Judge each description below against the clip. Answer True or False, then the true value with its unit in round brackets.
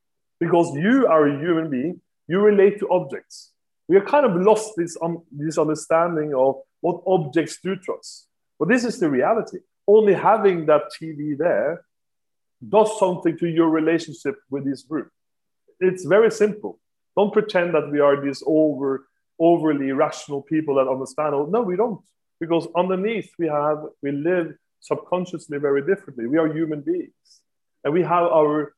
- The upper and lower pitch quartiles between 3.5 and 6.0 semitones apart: True (4.1 semitones)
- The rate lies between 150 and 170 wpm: True (165 wpm)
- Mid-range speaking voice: True (165 Hz)